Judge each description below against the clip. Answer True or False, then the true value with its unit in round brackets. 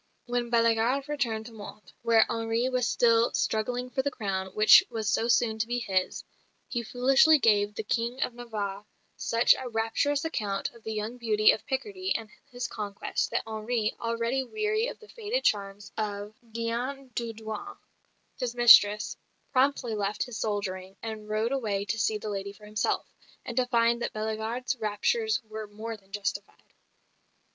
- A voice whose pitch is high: True (225 Hz)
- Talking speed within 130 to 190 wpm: True (165 wpm)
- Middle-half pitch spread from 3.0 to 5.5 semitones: False (2.6 semitones)